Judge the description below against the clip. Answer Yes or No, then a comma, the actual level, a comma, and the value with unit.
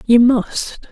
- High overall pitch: Yes, high, 235 Hz